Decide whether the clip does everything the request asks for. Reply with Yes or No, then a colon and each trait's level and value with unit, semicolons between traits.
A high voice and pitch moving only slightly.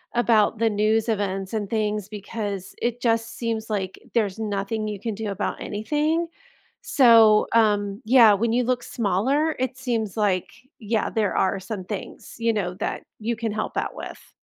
Yes: high, 220 Hz; narrow, 2.2 semitones